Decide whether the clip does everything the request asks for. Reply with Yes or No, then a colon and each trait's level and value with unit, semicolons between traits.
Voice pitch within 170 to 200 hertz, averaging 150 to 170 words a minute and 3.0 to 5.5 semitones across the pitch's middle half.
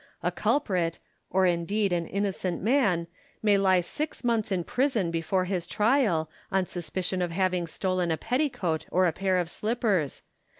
Yes: medium, 185 Hz; average, 155 wpm; average, 3.4 semitones